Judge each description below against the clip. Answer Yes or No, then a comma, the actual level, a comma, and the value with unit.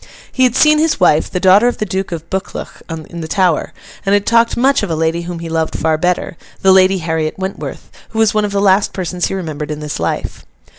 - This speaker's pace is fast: Yes, fast, 230 wpm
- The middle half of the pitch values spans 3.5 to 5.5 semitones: Yes, average, 4.0 semitones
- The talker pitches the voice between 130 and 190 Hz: Yes, medium, 185 Hz